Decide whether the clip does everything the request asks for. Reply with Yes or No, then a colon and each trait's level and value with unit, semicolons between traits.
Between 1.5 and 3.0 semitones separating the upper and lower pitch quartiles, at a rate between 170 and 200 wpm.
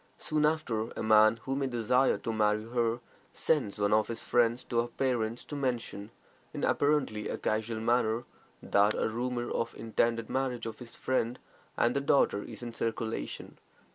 Yes: narrow, 2.4 semitones; average, 175 wpm